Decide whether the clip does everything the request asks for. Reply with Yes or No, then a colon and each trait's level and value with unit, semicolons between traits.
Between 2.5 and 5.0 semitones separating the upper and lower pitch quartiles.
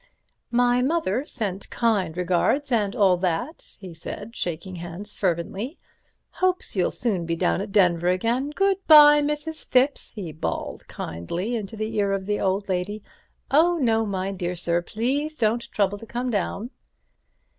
No: wide, 5.6 semitones